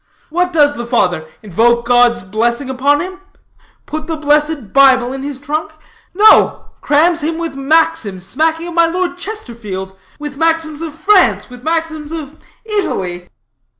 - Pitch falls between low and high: No, very high, 295 Hz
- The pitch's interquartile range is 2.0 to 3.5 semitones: No, average, 5.3 semitones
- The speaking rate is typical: Yes, average, 150 wpm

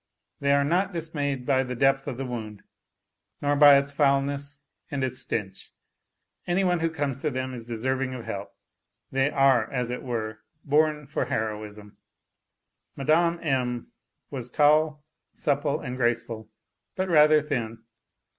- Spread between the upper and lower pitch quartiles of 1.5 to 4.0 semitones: Yes, average, 3.4 semitones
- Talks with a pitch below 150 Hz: Yes, low, 135 Hz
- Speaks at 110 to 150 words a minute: Yes, average, 145 wpm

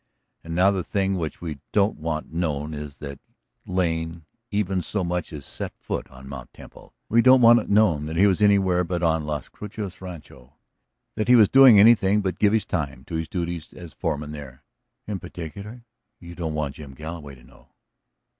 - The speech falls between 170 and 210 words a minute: Yes, average, 190 wpm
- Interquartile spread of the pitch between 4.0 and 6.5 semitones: Yes, average, 4.7 semitones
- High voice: No, very low, 85 Hz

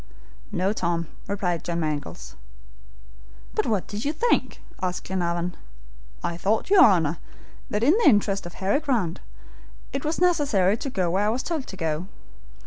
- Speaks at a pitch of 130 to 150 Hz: No, high, 195 Hz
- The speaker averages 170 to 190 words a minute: No, average, 160 wpm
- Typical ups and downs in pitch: No, wide, 6.8 semitones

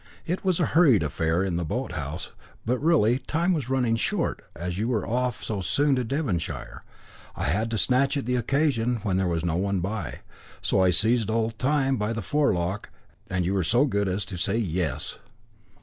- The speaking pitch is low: Yes, low, 110 Hz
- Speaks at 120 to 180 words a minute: No, average, 200 wpm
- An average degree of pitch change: No, wide, 6.2 semitones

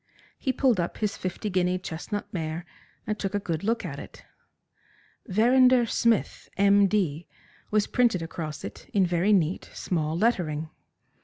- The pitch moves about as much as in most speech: Yes, average, 4.2 semitones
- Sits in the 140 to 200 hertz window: Yes, high, 190 Hz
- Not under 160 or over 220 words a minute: No, average, 150 wpm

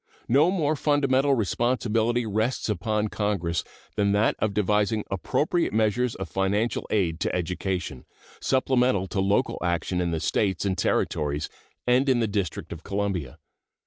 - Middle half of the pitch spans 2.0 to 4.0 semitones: No, average, 4.5 semitones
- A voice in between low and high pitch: No, low, 105 Hz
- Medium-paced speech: Yes, average, 145 wpm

